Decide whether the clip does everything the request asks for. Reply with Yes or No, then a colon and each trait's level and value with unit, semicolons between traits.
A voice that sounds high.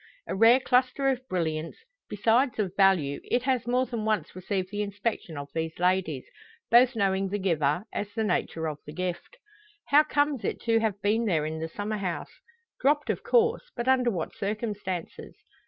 Yes: high, 205 Hz